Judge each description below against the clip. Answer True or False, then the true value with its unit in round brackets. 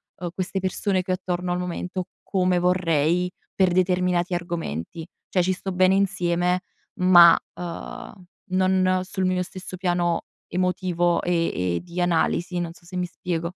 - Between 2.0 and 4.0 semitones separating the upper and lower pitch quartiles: False (1.1 semitones)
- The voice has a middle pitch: True (180 Hz)